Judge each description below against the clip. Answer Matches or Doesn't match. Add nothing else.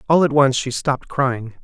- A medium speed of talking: Doesn't match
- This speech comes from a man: Matches